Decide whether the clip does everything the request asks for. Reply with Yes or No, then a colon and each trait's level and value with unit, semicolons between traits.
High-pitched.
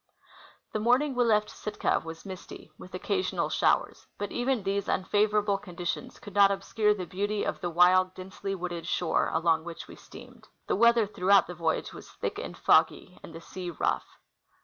Yes: high, 195 Hz